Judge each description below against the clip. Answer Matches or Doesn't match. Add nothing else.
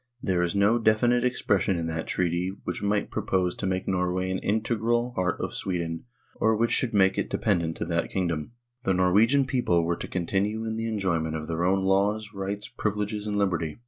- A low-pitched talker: Matches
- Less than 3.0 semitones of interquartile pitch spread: Doesn't match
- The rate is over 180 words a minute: Matches